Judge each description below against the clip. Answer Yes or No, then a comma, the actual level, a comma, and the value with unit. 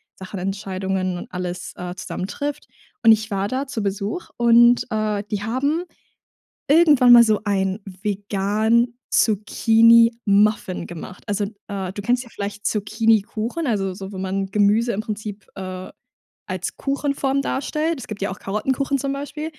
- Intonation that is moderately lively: Yes, average, 3.7 semitones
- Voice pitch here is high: Yes, high, 215 Hz